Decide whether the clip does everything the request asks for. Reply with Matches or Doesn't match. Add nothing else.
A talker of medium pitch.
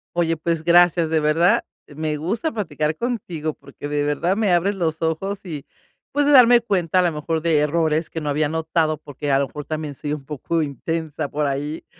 Matches